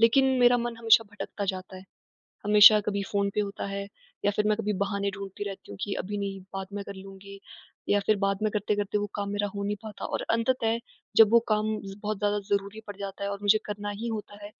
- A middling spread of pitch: No, narrow, 1.2 semitones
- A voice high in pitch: Yes, high, 205 Hz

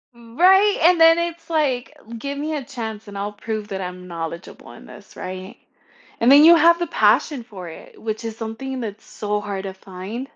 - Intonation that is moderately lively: No, wide, 6.9 semitones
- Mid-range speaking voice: No, high, 230 Hz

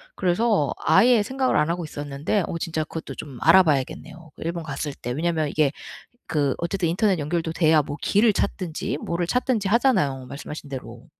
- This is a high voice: No, medium, 165 Hz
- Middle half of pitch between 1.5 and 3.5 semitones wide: No, average, 4.4 semitones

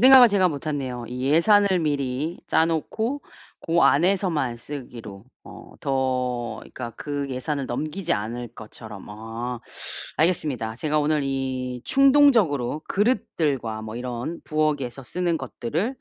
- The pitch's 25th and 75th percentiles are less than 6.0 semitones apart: Yes, wide, 5.5 semitones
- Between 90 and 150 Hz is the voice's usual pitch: Yes, medium, 140 Hz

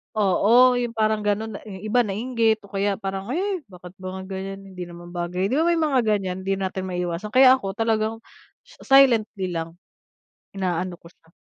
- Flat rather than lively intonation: No, average, 3.7 semitones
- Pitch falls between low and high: No, high, 195 Hz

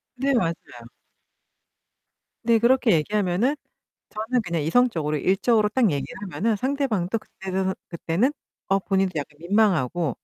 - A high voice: Yes, high, 195 Hz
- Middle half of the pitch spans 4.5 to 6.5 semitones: Yes, wide, 5.4 semitones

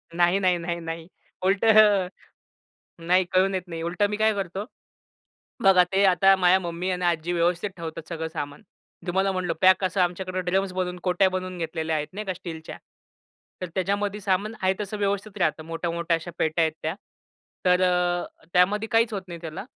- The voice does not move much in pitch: Yes, narrow, 2.2 semitones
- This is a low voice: No, medium, 180 Hz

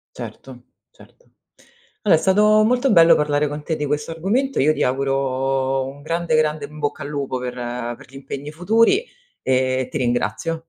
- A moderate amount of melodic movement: Yes, average, 3.9 semitones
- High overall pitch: No, medium, 150 Hz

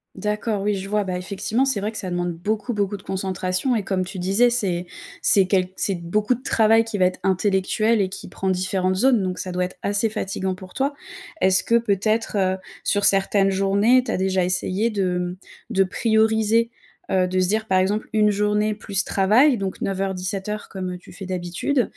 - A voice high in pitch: Yes, high, 195 Hz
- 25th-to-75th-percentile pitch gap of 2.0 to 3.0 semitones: Yes, narrow, 2.5 semitones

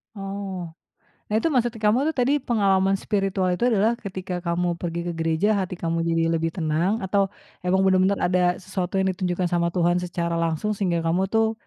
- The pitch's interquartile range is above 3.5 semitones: No, average, 2.8 semitones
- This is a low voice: No, medium, 185 Hz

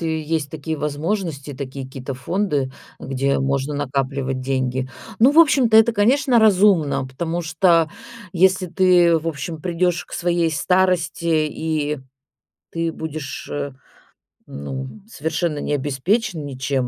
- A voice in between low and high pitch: Yes, medium, 160 Hz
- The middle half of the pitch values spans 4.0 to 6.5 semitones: Yes, average, 4.5 semitones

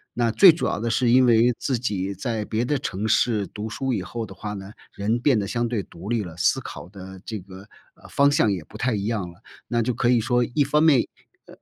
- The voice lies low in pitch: Yes, low, 110 Hz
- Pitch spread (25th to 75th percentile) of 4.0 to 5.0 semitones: No, average, 3.5 semitones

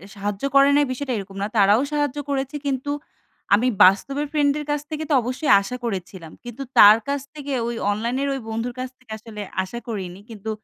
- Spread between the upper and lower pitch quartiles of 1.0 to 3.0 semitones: No, wide, 5.4 semitones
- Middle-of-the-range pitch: No, high, 245 Hz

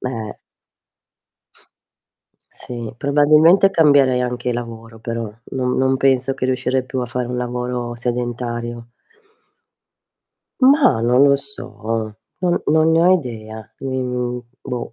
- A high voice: No, low, 125 Hz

